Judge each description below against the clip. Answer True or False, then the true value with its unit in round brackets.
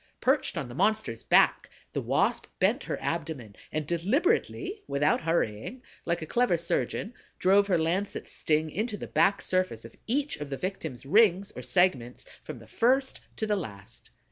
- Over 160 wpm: True (170 wpm)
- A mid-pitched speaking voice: True (175 Hz)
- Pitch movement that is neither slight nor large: False (6.5 semitones)